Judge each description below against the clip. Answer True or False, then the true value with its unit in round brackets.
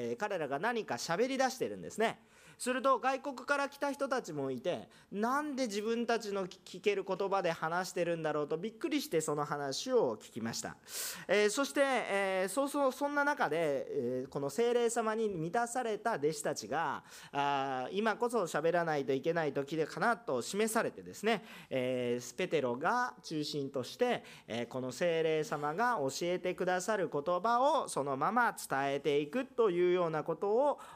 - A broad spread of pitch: True (8.0 semitones)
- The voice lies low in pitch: False (195 Hz)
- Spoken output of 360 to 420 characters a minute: False (335 characters per minute)